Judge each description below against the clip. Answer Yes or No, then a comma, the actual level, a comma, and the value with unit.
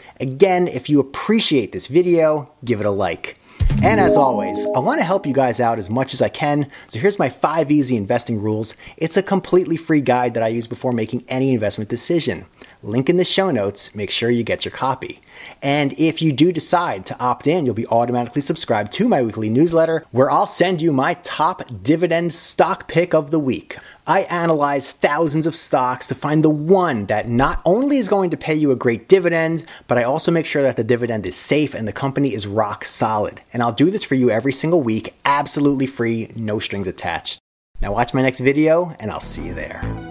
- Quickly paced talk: Yes, fast, 215 wpm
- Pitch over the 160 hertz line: No, medium, 140 Hz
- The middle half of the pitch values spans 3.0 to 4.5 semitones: No, wide, 5.4 semitones